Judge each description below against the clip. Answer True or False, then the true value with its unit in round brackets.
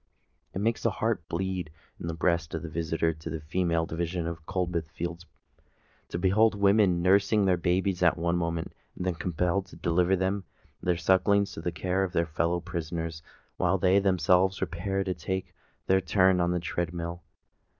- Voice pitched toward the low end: True (90 Hz)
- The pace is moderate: True (180 wpm)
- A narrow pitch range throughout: True (2.1 semitones)